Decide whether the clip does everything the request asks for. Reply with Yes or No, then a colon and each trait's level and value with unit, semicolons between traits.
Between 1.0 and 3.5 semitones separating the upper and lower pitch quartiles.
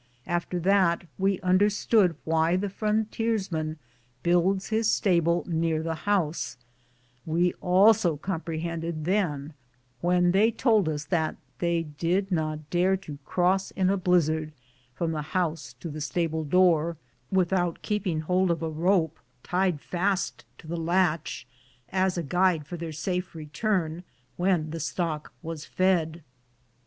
Yes: average, 2.8 semitones